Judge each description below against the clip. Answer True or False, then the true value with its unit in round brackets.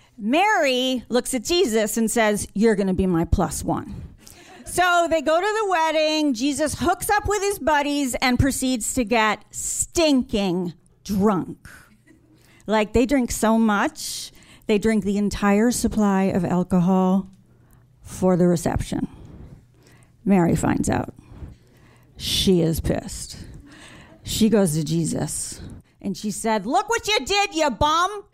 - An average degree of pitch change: False (8.0 semitones)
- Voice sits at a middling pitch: False (225 Hz)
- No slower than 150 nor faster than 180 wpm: False (140 wpm)